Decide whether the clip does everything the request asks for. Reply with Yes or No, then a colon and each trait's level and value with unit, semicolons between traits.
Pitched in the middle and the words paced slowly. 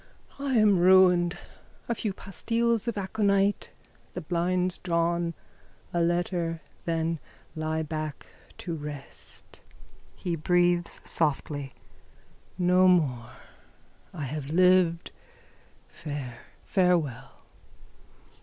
Yes: medium, 175 Hz; slow, 95 wpm